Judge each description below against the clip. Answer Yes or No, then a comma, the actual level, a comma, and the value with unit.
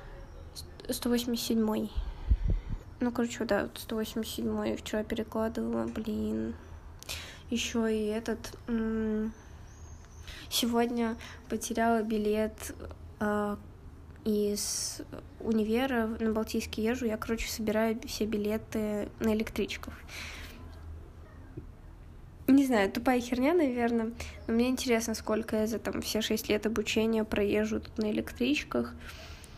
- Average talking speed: No, slow, 95 wpm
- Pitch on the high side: Yes, high, 215 Hz